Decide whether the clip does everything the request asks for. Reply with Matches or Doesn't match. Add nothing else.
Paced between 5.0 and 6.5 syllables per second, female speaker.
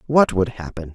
Doesn't match